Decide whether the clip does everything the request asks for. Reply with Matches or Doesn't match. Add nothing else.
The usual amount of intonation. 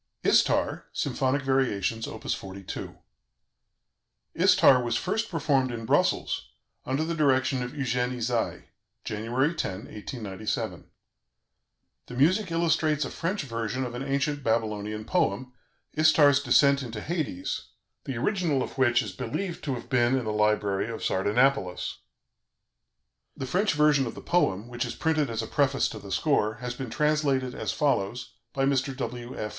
Matches